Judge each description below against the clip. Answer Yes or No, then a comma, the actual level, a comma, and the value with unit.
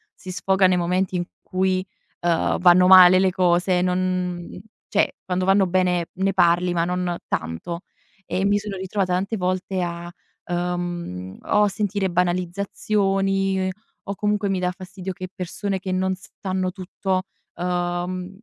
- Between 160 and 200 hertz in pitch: Yes, medium, 185 Hz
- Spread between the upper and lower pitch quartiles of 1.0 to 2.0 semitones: Yes, narrow, 1.4 semitones